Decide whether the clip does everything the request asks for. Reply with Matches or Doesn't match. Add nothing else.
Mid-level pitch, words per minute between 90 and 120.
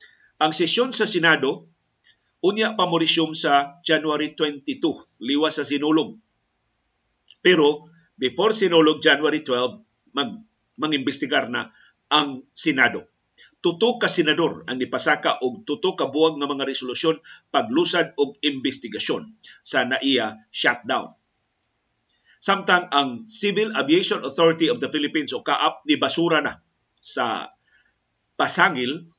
Matches